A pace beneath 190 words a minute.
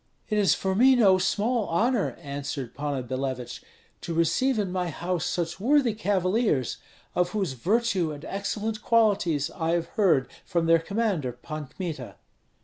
Yes: average, 150 wpm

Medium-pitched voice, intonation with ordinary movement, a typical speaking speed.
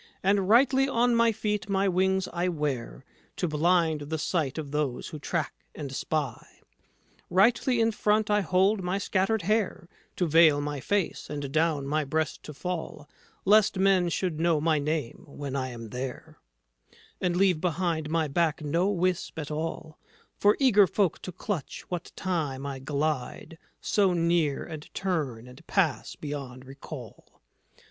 Yes: medium, 165 Hz; average, 4.5 semitones; average, 155 wpm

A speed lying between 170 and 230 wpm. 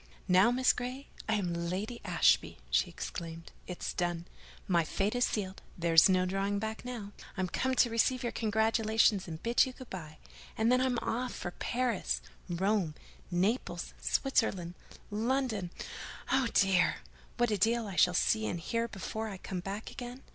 No: average, 160 wpm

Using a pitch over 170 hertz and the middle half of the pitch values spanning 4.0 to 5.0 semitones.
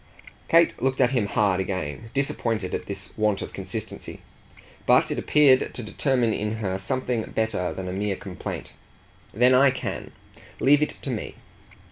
No: low, 110 Hz; average, 4.7 semitones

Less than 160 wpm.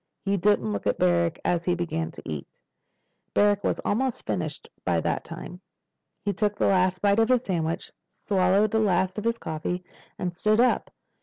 No: average, 180 wpm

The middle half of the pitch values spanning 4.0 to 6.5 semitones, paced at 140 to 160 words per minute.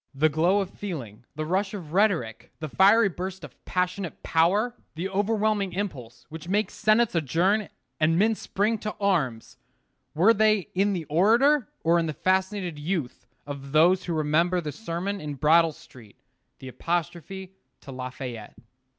Yes: average, 4.7 semitones; average, 155 wpm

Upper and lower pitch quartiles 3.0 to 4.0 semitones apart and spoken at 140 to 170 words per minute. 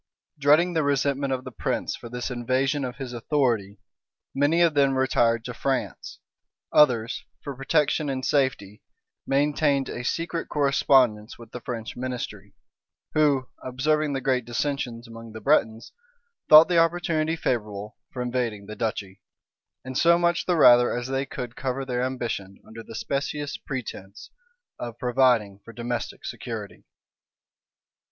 Yes: average, 3.4 semitones; average, 145 wpm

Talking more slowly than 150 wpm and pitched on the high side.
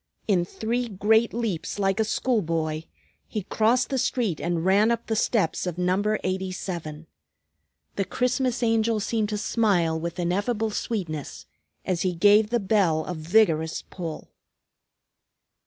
Yes: average, 140 wpm; high, 200 Hz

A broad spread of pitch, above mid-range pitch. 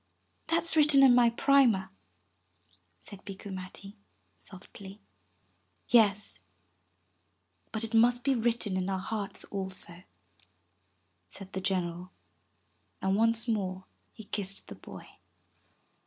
No: average, 3.7 semitones; high, 205 Hz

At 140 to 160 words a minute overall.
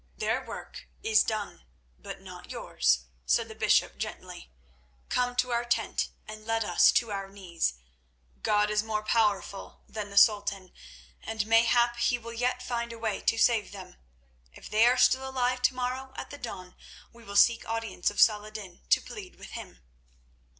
No: average, 170 wpm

